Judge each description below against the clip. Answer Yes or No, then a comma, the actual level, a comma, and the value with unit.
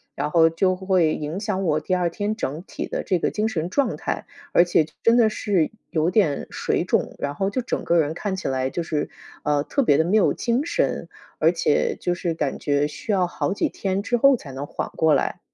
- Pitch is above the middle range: No, medium, 180 Hz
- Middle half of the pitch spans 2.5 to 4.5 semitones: No, average, 5.1 semitones